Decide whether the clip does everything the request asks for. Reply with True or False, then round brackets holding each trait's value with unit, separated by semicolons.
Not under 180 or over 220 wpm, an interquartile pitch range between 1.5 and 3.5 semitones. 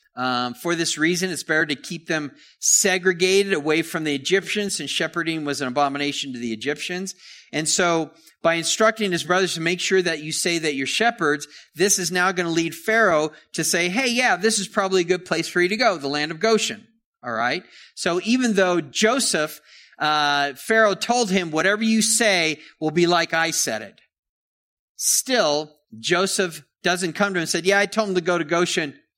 False (200 wpm; 3.9 semitones)